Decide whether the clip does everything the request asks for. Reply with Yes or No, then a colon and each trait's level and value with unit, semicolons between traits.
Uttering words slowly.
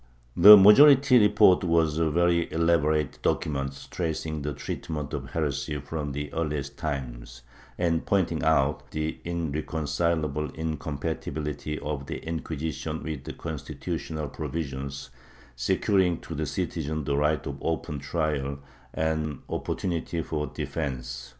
Yes: slow, 125 wpm